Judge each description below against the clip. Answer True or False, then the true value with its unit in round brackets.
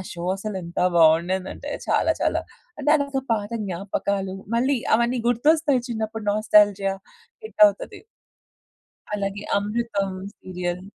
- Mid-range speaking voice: False (205 Hz)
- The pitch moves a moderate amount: True (3.8 semitones)